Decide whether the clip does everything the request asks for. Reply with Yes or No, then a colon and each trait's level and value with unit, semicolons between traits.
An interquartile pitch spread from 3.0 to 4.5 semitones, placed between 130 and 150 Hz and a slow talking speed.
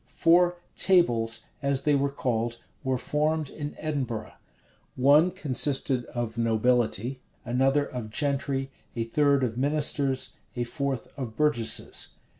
Yes: average, 3.5 semitones; low, 135 Hz; slow, 120 wpm